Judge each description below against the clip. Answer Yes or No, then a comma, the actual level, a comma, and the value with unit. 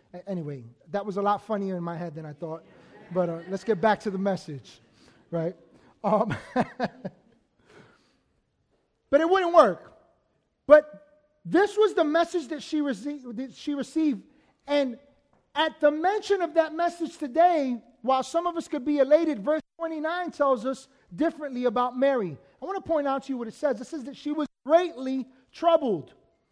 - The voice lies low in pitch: No, very high, 275 Hz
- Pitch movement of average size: No, wide, 7.3 semitones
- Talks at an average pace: Yes, average, 170 wpm